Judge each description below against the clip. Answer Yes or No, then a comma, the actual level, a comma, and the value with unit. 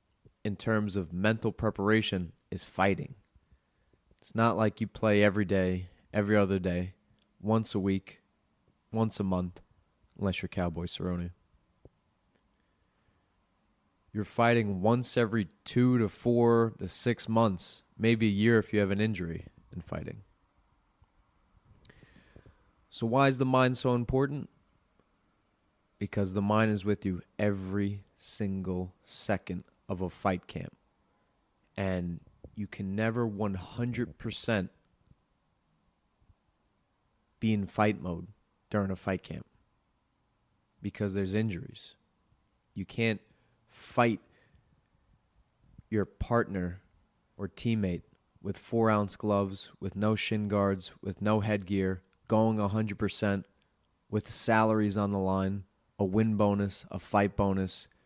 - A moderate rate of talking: No, slow, 120 wpm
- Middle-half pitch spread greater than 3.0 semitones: No, narrow, 2.6 semitones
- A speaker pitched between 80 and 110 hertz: Yes, low, 100 Hz